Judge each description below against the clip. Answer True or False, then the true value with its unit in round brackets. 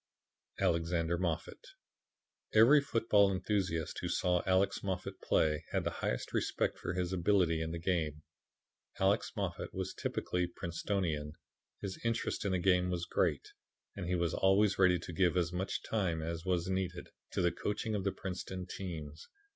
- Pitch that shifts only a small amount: True (2.3 semitones)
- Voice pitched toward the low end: True (90 Hz)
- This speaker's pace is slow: False (160 wpm)